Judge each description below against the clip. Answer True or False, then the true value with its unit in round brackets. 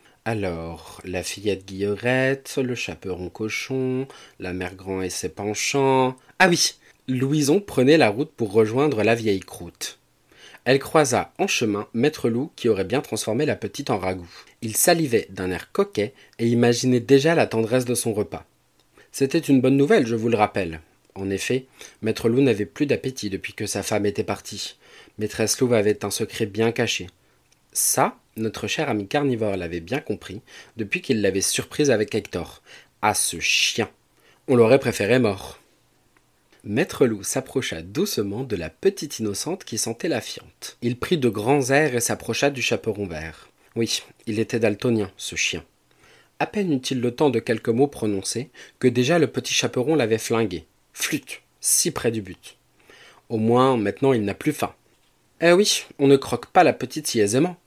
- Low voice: True (115 Hz)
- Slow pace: False (175 wpm)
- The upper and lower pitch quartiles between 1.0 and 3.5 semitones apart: False (4.5 semitones)